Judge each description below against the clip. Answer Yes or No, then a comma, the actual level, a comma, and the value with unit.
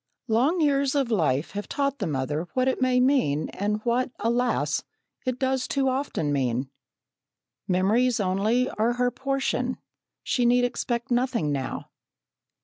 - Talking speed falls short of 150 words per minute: Yes, average, 140 wpm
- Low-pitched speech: No, high, 245 Hz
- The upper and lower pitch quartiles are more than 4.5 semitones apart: Yes, wide, 5.6 semitones